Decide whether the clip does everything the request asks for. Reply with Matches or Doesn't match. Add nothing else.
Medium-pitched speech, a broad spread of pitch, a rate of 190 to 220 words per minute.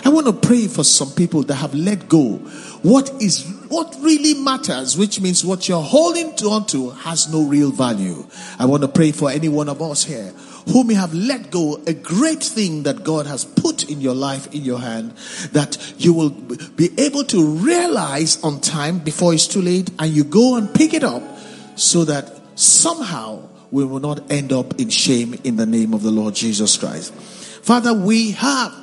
Matches